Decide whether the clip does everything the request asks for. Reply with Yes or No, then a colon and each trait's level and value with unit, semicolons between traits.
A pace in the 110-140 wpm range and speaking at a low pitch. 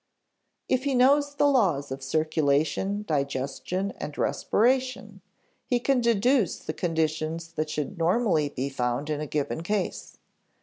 No: slow, 135 wpm; medium, 165 Hz